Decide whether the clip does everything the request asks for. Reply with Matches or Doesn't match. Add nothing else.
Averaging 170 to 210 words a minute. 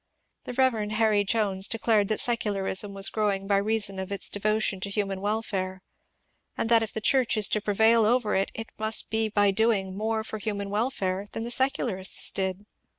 Matches